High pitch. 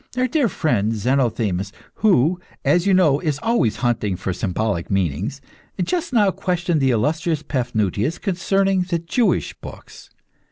No: medium, 145 Hz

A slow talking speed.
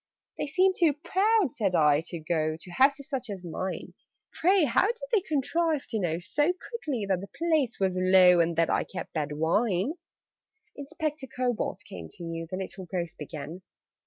No: average, 185 wpm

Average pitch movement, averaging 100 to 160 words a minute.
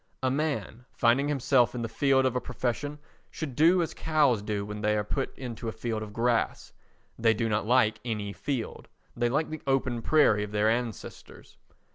No: average, 3.8 semitones; average, 190 wpm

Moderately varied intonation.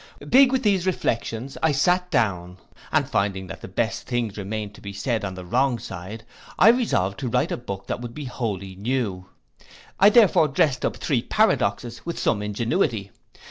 No: wide, 6.5 semitones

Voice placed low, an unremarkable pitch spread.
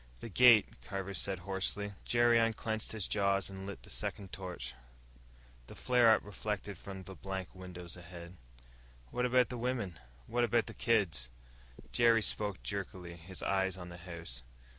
Yes: low, 100 Hz; average, 3.7 semitones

